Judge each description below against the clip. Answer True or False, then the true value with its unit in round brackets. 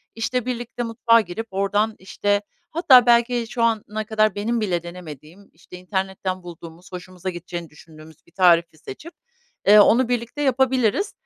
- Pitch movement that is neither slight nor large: True (4.8 semitones)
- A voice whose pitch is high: True (205 Hz)